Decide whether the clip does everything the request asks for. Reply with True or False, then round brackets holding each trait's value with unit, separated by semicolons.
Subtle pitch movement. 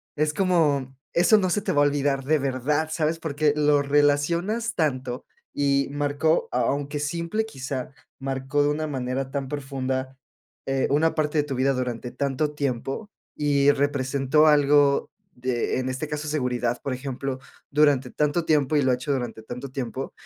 True (2.2 semitones)